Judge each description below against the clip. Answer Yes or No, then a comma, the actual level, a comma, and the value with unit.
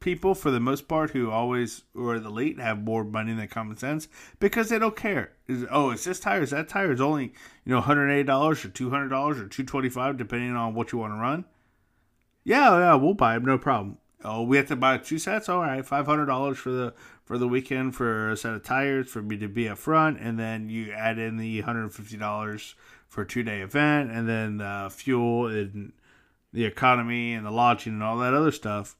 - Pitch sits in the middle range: No, low, 120 Hz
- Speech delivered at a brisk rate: Yes, fast, 215 wpm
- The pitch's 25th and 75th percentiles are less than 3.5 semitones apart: No, average, 3.9 semitones